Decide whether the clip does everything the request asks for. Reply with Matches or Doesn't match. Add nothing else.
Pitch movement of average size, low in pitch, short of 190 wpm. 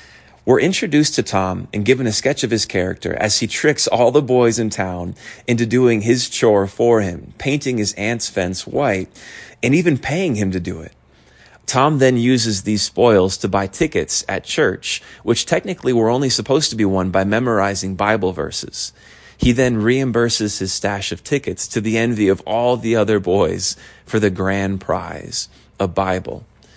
Matches